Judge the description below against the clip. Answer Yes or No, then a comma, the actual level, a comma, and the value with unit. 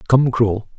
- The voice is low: Yes, low, 120 Hz